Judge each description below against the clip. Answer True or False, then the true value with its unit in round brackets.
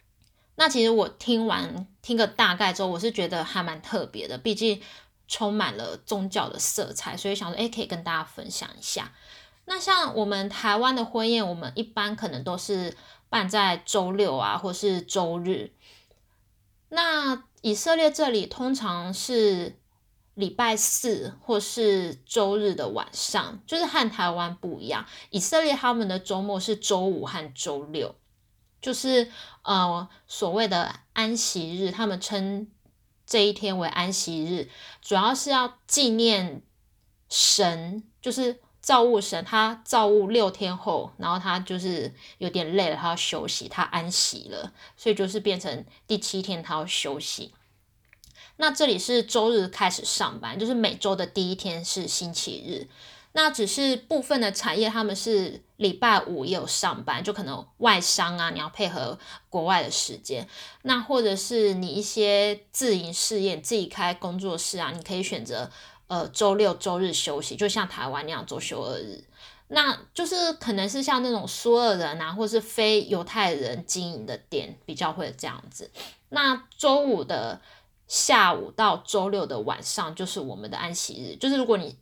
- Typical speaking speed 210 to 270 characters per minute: True (240 characters per minute)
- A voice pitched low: False (205 Hz)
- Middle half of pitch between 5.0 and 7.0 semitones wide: False (4.1 semitones)